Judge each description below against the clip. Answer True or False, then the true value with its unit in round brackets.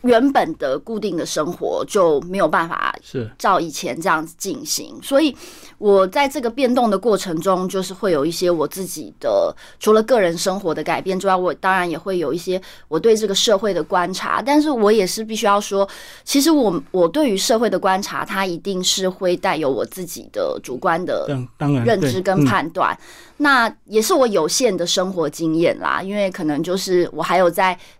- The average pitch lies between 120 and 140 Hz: False (195 Hz)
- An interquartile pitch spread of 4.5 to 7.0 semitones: True (5.4 semitones)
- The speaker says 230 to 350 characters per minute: True (285 characters per minute)